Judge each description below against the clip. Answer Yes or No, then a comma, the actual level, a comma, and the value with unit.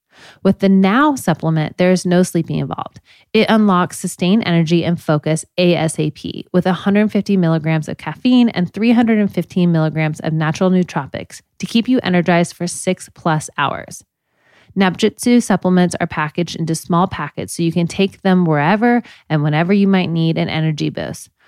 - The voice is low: No, medium, 175 Hz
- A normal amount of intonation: Yes, average, 3.4 semitones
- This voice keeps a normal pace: Yes, average, 155 wpm